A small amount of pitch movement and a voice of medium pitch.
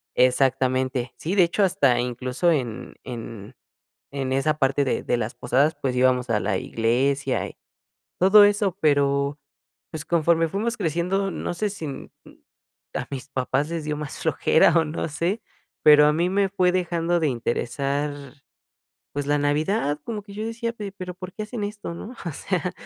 No: wide, 5.5 semitones; medium, 150 Hz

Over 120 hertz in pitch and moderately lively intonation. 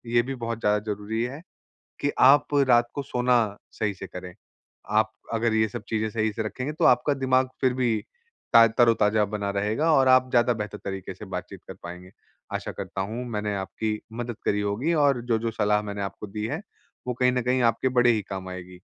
No: low, 115 Hz; average, 3.2 semitones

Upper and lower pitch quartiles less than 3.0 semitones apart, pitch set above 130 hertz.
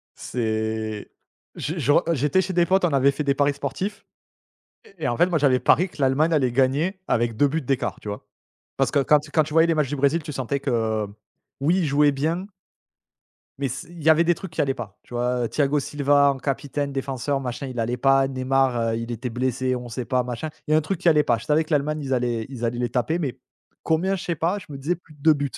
No: average, 3.9 semitones; medium, 140 Hz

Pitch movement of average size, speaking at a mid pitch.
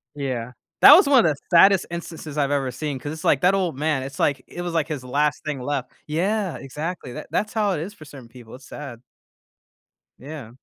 Yes: average, 4.4 semitones; medium, 150 Hz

